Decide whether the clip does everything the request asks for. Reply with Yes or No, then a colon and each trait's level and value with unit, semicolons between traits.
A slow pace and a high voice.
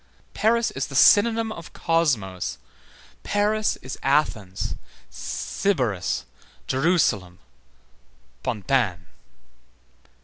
No: slow, 70 wpm; low, 135 Hz